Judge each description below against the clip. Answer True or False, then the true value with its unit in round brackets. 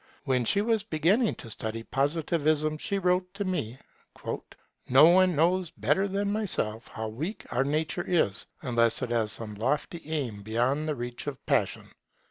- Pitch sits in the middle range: True (150 Hz)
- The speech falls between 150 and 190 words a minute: True (160 wpm)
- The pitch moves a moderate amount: False (7.3 semitones)